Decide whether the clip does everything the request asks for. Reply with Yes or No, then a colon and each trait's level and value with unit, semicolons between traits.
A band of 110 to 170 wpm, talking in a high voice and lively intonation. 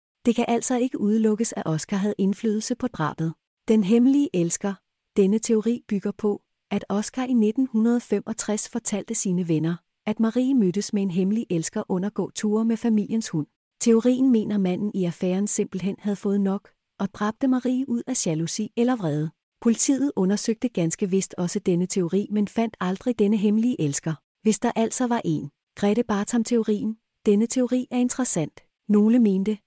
No: average, 160 wpm; high, 210 Hz; average, 3.2 semitones